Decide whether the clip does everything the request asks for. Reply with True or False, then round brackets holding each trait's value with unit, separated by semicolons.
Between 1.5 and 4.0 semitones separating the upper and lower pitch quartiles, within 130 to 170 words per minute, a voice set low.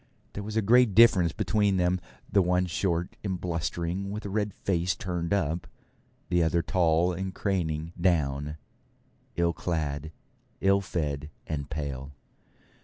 True (3.5 semitones; 140 wpm; 90 Hz)